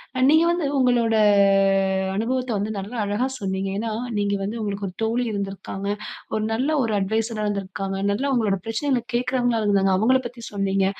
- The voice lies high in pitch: Yes, high, 220 Hz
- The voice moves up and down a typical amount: Yes, average, 3.7 semitones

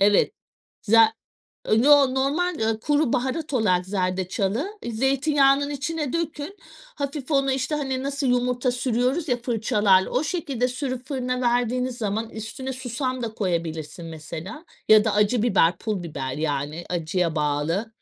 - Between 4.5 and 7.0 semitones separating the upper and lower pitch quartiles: Yes, wide, 5.4 semitones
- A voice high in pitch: Yes, high, 245 Hz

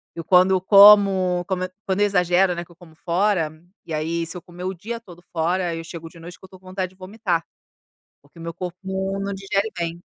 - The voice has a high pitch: No, medium, 180 Hz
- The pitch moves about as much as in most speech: No, narrow, 2.2 semitones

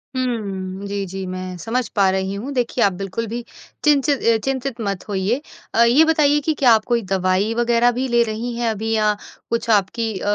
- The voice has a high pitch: Yes, high, 225 Hz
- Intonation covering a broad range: No, average, 3.6 semitones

